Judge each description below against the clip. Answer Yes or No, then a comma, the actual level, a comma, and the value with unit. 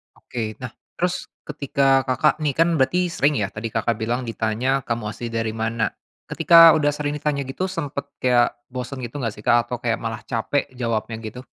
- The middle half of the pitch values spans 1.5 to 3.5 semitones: No, average, 4.1 semitones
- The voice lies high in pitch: No, low, 125 Hz